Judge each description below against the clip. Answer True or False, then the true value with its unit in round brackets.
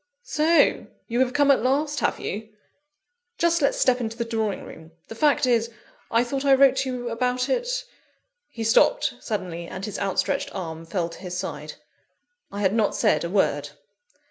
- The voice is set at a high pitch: True (235 Hz)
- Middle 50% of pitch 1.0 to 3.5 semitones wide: False (5.6 semitones)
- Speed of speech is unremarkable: True (185 wpm)